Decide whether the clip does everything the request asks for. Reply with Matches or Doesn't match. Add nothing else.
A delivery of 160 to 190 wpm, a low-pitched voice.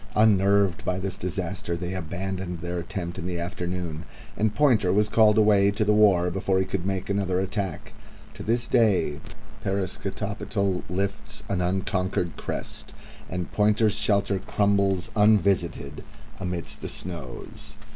Doesn't match